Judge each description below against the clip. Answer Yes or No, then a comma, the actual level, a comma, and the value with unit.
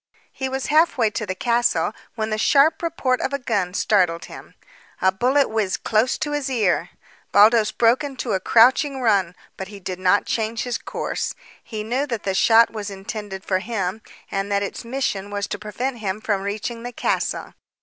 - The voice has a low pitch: No, high, 220 Hz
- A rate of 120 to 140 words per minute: No, average, 190 wpm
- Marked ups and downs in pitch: No, average, 4.0 semitones